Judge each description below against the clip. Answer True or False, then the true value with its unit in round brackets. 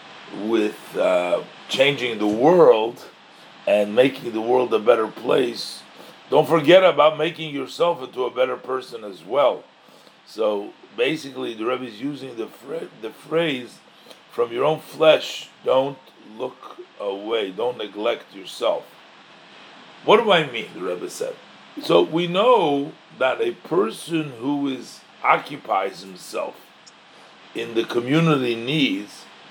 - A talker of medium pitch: True (155 Hz)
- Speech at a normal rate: False (130 wpm)